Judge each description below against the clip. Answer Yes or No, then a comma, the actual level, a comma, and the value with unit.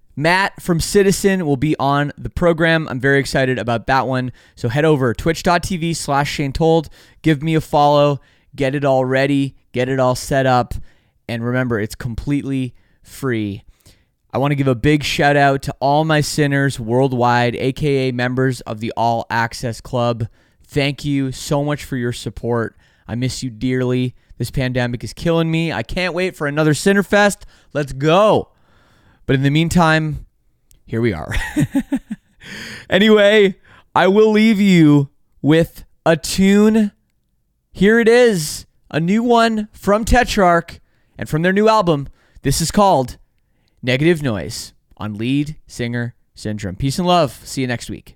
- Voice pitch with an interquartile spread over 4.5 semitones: Yes, average, 5.3 semitones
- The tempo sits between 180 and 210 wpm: No, average, 160 wpm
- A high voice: No, medium, 140 Hz